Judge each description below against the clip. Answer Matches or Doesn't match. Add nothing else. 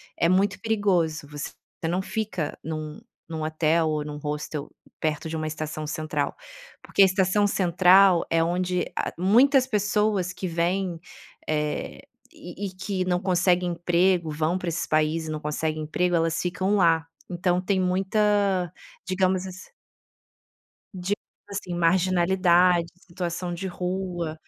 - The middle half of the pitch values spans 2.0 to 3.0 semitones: Matches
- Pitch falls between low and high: Matches